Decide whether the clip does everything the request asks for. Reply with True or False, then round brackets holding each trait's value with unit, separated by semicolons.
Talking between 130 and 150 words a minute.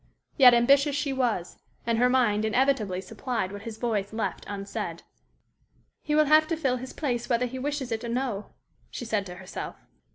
False (185 wpm)